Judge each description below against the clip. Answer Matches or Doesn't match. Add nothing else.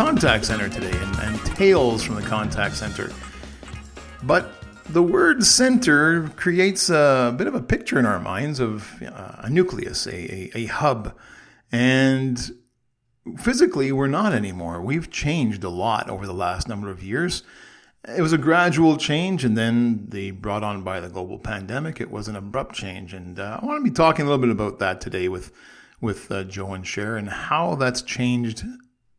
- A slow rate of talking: Doesn't match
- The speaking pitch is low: Matches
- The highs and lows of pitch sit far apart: Matches